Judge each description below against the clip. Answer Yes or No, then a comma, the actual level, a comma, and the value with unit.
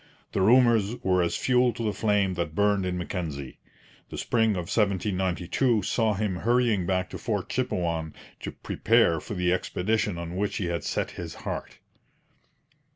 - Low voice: Yes, very low, 95 Hz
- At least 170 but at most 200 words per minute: No, average, 160 wpm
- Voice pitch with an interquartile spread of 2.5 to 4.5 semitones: Yes, average, 3.8 semitones